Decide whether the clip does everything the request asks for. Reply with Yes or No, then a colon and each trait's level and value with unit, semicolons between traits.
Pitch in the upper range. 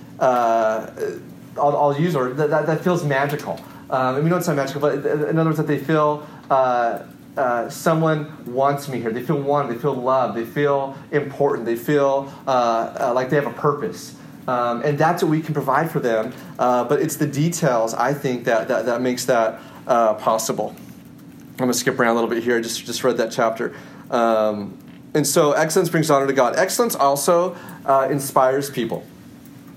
No: medium, 140 Hz